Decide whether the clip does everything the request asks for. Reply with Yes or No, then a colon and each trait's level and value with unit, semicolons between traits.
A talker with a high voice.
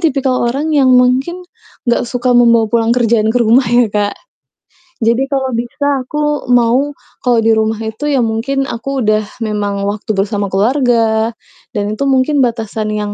Yes: high, 235 Hz